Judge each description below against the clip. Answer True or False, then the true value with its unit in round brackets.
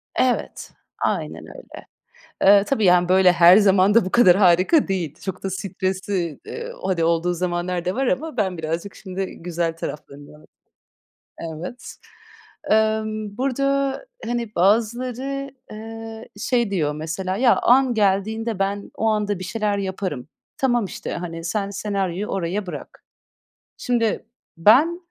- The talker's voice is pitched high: True (200 Hz)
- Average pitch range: True (4.3 semitones)